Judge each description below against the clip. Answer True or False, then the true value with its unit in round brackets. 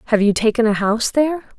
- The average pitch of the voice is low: False (230 Hz)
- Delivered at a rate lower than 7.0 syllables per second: False (7.5 syllables/s)